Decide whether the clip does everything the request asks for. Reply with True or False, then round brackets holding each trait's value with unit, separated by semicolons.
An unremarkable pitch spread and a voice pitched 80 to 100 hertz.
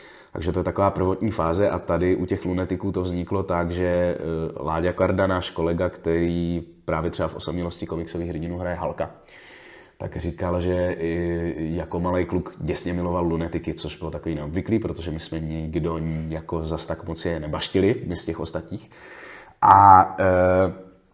False (1.6 semitones; 85 Hz)